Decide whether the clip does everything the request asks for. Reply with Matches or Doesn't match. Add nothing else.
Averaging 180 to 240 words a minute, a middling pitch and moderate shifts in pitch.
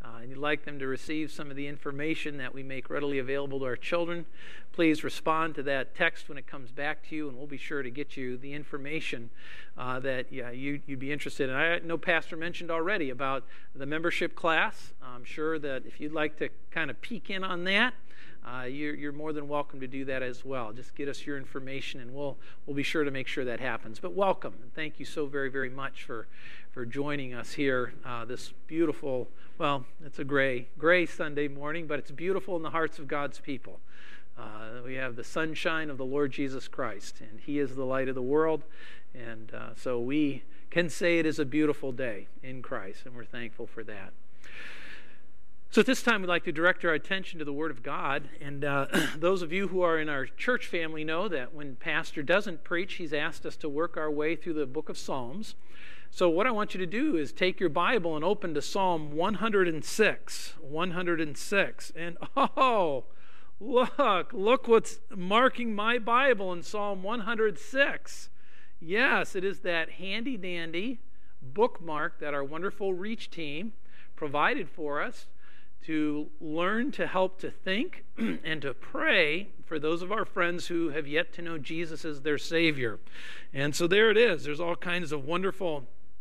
Matches